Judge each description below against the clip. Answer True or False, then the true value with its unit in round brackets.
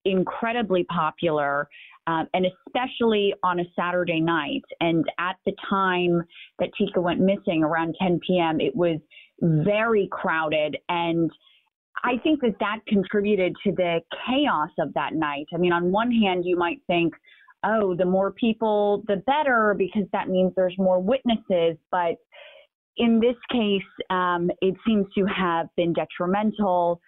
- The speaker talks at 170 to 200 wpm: False (150 wpm)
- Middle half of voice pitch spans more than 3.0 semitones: True (3.6 semitones)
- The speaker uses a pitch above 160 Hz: True (185 Hz)